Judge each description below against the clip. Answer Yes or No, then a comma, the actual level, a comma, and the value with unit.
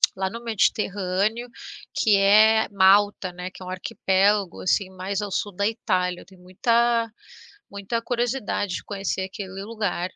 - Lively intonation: No, average, 2.7 semitones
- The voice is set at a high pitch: Yes, high, 200 Hz